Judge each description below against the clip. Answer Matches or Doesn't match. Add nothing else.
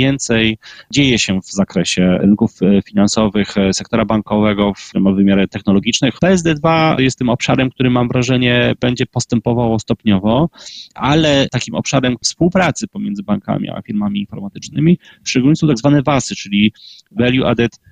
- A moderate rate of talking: Matches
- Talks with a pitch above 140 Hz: Doesn't match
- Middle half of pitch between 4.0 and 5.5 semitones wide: Matches